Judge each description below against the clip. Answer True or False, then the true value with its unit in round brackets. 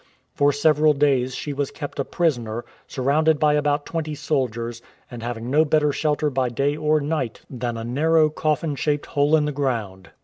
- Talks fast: False (180 wpm)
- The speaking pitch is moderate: True (145 Hz)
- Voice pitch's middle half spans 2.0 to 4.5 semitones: True (3.4 semitones)